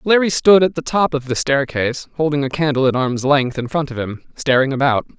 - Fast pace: Yes, fast, 230 wpm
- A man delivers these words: Yes, male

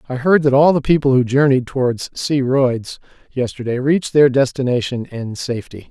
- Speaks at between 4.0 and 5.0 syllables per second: No, 5.2 syllables/s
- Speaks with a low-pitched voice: Yes, low, 130 Hz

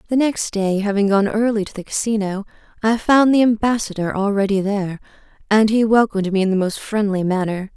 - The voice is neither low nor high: No, high, 210 Hz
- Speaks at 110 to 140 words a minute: No, average, 185 wpm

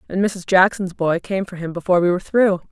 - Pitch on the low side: No, medium, 185 Hz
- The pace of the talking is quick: Yes, fast, 245 wpm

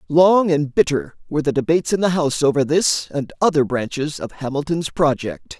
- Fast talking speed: No, average, 180 wpm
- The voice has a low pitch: No, medium, 150 Hz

